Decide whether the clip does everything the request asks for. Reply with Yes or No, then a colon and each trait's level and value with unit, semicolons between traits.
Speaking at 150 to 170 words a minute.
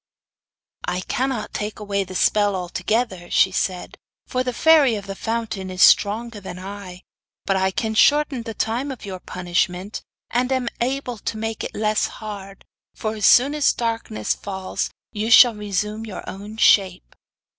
Yes: average, 165 wpm